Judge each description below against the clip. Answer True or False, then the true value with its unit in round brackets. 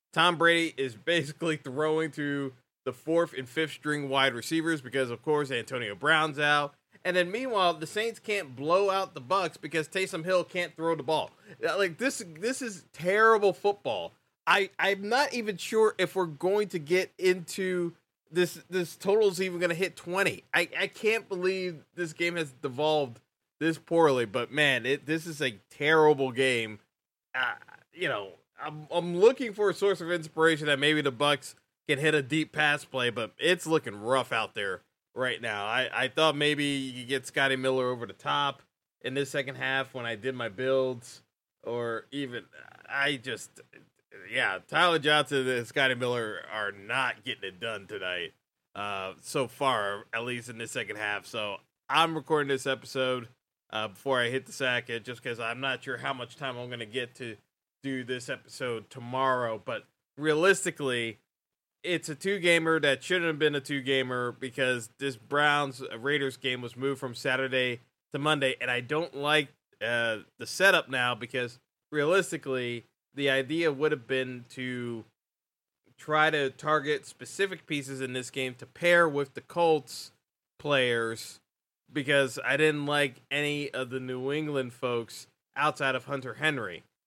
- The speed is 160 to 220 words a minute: True (170 wpm)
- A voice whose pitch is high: False (145 Hz)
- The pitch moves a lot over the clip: False (4.4 semitones)